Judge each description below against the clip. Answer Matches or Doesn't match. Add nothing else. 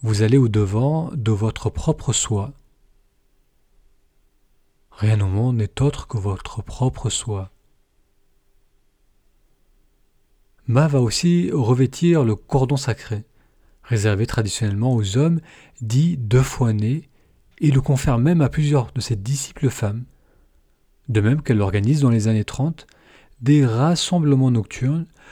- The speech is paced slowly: Matches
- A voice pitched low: Matches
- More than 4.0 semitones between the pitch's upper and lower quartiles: Matches